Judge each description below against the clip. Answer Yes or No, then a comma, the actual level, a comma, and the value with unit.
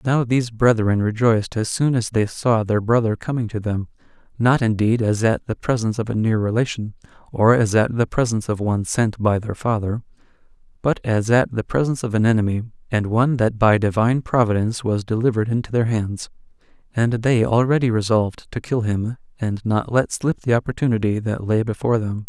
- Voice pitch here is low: Yes, low, 115 Hz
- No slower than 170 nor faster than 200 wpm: Yes, average, 190 wpm